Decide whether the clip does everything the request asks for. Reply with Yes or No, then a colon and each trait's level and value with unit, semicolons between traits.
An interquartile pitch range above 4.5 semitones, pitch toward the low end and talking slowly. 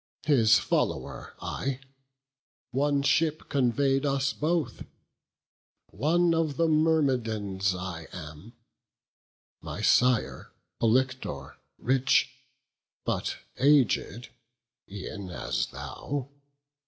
Yes: average, 4.9 semitones; low, 130 Hz; slow, 80 wpm